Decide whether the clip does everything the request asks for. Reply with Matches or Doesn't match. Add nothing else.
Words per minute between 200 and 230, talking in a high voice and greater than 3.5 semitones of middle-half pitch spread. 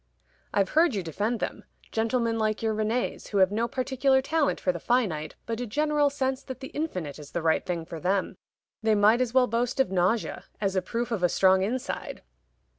Matches